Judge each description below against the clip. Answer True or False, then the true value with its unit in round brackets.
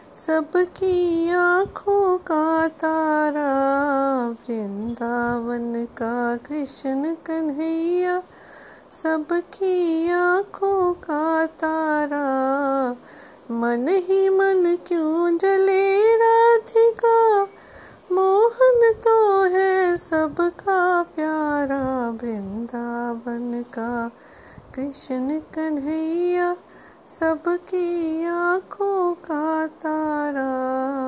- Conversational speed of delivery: False (60 wpm)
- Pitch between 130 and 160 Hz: False (320 Hz)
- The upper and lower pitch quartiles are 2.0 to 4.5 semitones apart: False (5.0 semitones)